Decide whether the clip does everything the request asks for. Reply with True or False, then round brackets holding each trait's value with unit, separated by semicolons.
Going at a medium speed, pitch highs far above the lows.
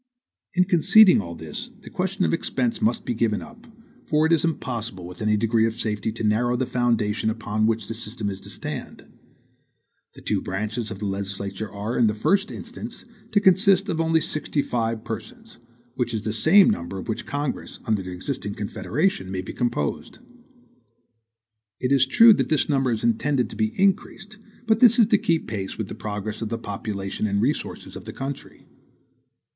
True (190 wpm; 7.5 semitones)